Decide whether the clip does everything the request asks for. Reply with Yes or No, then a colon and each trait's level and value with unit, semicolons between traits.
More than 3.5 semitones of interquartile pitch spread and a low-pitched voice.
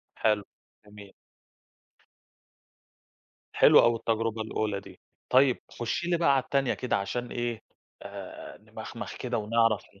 No: average, 2.8 semitones; low, 115 Hz